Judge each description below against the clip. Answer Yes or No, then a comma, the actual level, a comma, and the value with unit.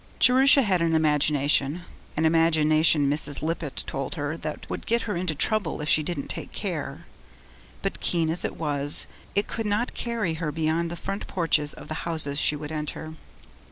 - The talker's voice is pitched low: No, medium, 160 Hz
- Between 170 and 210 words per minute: Yes, average, 180 wpm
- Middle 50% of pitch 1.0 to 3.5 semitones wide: Yes, average, 2.8 semitones